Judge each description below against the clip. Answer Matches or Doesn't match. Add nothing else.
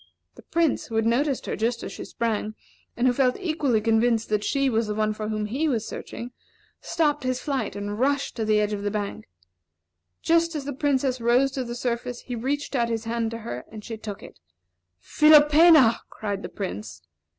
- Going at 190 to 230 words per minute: Matches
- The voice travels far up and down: Doesn't match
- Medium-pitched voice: Doesn't match